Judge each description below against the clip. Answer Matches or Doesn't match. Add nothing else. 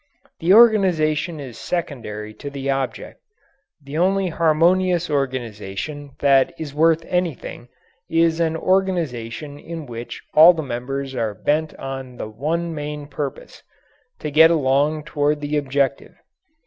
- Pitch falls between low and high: Matches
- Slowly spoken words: Matches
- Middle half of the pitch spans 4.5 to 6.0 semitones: Doesn't match